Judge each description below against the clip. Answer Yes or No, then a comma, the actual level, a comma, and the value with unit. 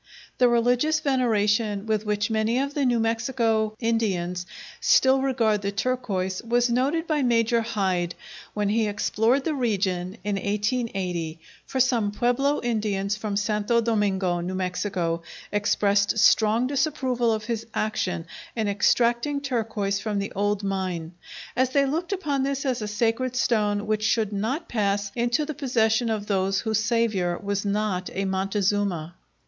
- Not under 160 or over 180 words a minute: No, average, 150 wpm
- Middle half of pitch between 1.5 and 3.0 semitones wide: No, average, 3.4 semitones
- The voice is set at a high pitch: Yes, high, 215 Hz